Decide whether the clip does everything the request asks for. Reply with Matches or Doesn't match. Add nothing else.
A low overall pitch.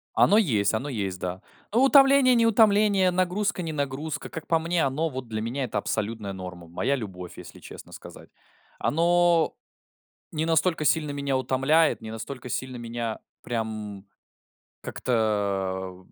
Matches